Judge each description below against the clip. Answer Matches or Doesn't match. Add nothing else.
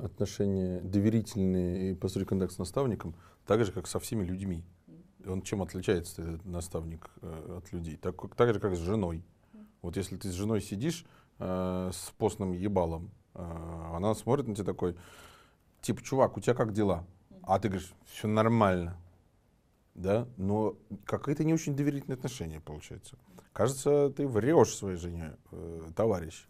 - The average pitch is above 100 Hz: Doesn't match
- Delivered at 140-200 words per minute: Matches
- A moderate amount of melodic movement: Matches